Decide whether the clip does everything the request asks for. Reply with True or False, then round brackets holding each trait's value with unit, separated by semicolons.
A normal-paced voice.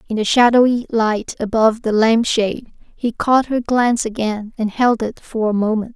True (180 wpm)